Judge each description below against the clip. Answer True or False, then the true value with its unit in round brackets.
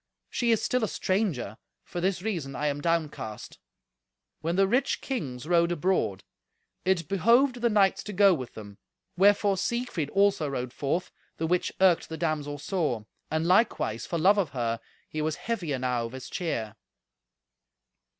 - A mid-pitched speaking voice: True (170 Hz)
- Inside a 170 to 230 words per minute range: False (160 wpm)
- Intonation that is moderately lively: False (5.9 semitones)